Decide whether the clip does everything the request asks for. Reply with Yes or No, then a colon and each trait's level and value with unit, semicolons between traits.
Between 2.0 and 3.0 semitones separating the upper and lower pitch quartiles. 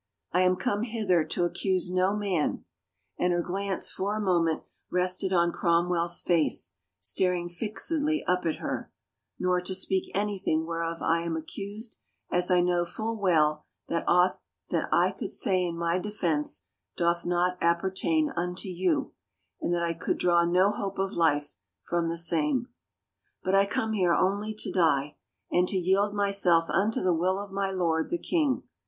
Yes: narrow, 2.6 semitones